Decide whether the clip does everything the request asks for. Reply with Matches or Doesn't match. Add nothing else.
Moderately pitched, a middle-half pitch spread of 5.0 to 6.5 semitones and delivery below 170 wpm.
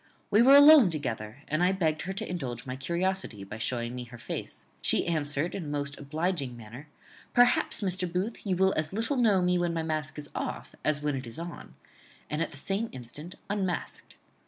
Doesn't match